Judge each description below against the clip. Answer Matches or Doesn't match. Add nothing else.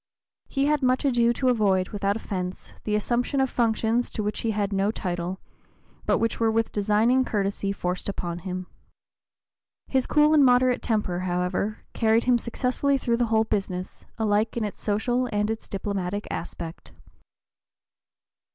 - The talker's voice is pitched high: Matches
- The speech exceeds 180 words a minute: Doesn't match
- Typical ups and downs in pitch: Matches